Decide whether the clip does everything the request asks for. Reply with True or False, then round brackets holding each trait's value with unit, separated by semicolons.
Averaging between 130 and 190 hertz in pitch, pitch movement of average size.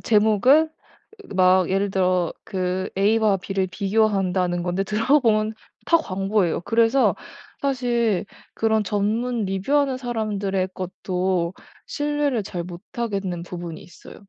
False (200 Hz; 3.6 semitones)